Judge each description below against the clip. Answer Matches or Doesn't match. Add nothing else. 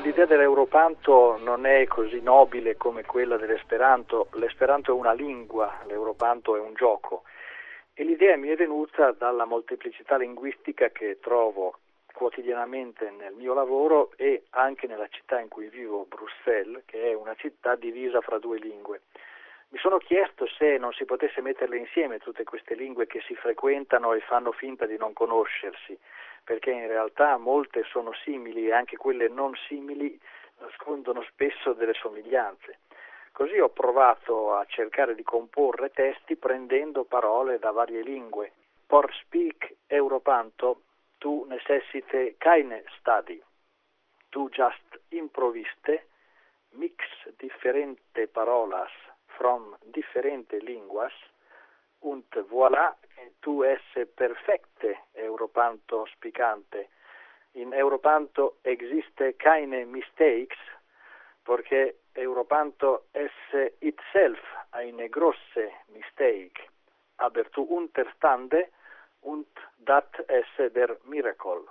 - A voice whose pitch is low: Doesn't match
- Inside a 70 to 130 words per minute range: Matches